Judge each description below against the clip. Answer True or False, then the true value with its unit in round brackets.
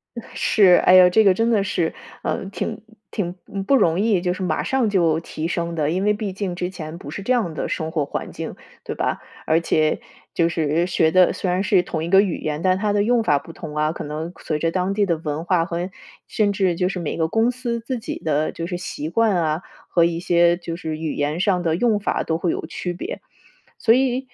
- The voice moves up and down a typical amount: True (3.8 semitones)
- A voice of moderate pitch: True (180 Hz)